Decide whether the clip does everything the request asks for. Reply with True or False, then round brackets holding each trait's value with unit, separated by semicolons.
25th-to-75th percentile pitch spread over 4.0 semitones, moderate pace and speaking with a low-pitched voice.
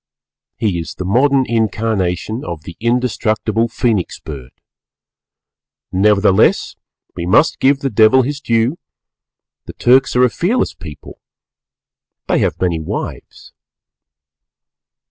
False (5.4 semitones; 115 wpm; 110 Hz)